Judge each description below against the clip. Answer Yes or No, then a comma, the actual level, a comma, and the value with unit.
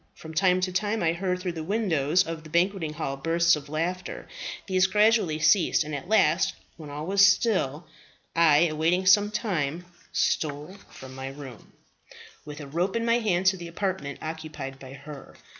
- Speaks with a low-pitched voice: No, medium, 170 Hz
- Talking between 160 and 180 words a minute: Yes, average, 175 wpm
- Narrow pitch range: No, average, 3.8 semitones